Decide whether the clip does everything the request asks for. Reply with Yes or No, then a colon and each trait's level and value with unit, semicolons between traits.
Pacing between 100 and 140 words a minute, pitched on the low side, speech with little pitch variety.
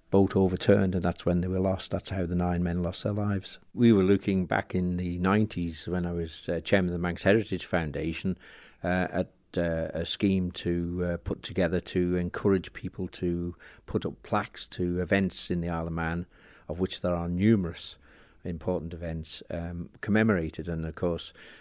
No: average, 190 wpm; very low, 90 Hz; narrow, 1.9 semitones